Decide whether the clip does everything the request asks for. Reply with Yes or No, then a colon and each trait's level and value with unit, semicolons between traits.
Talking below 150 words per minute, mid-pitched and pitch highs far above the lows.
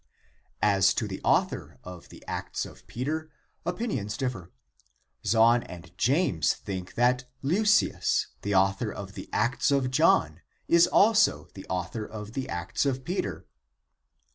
No: average, 140 wpm; low, 115 Hz; wide, 6.4 semitones